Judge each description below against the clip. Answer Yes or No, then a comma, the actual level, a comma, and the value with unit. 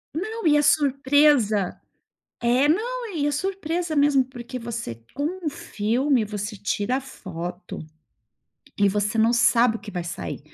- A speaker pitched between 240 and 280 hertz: Yes, very high, 250 Hz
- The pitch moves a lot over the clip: Yes, wide, 5.9 semitones